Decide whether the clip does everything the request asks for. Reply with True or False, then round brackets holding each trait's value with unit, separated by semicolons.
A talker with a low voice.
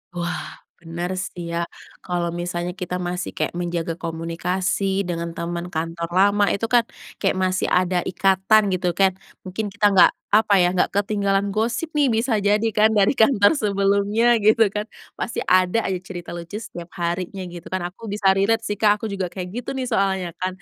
False (190 Hz)